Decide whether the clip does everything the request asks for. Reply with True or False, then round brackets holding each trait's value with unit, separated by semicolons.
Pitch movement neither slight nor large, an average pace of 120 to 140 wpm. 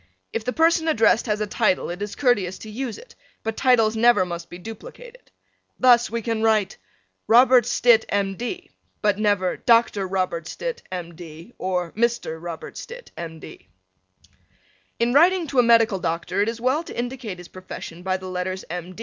False (5.0 semitones; 180 wpm)